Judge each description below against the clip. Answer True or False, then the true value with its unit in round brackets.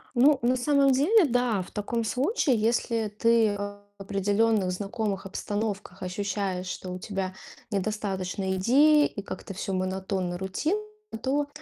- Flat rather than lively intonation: False (4.3 semitones)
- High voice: True (205 Hz)